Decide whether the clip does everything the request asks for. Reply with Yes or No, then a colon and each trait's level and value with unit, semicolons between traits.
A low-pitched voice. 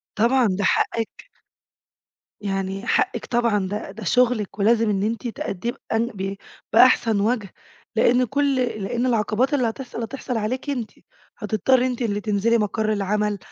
No: high, 225 Hz